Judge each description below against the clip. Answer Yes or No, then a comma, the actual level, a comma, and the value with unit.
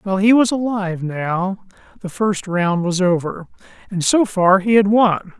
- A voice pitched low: No, high, 195 Hz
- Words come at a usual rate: Yes, average, 180 wpm